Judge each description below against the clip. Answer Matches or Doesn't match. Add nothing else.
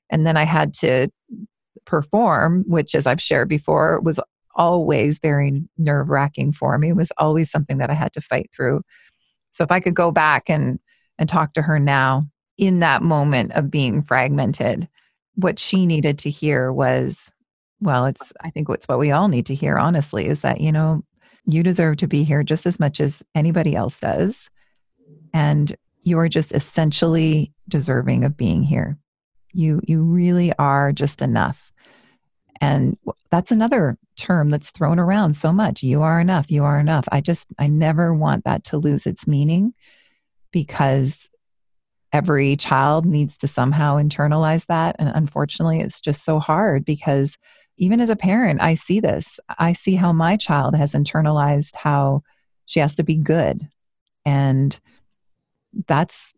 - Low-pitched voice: Doesn't match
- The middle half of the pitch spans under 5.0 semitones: Matches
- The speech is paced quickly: Doesn't match